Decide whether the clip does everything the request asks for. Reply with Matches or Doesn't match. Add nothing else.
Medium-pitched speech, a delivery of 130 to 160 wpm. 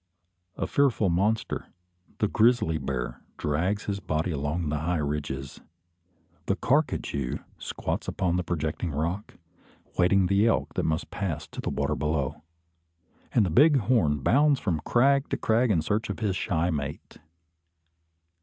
Doesn't match